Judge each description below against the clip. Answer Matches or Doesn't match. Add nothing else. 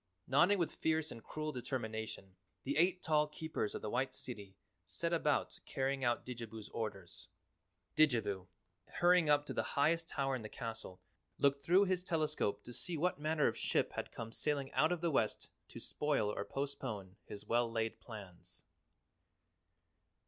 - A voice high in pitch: Doesn't match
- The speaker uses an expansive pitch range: Matches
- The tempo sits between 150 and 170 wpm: Matches